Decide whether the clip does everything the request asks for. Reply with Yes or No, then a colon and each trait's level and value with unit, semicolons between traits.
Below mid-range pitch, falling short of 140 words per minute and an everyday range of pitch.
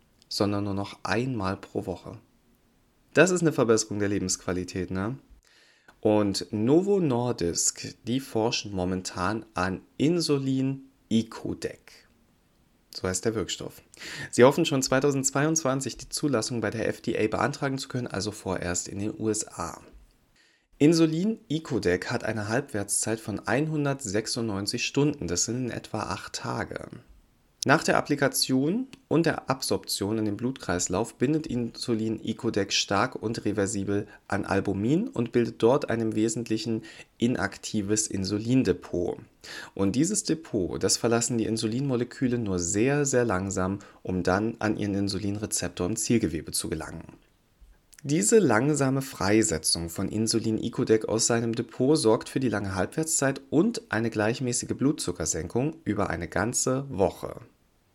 Yes: low, 110 Hz; slow, 125 wpm; average, 4.7 semitones